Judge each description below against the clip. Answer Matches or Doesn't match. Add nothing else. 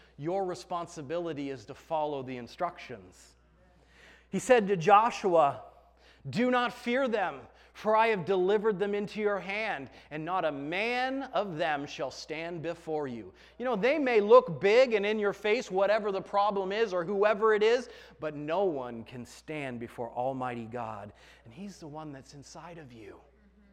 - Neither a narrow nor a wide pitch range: Doesn't match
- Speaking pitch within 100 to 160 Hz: Doesn't match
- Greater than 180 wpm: Doesn't match